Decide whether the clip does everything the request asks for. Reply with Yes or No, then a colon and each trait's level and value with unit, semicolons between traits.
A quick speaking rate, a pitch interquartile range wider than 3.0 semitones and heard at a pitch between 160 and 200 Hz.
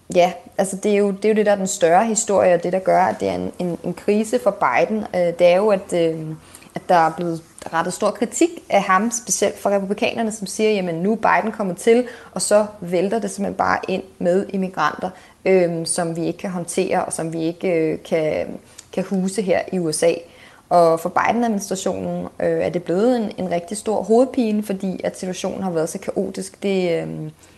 No: average, 215 wpm; average, 3.6 semitones; medium, 185 Hz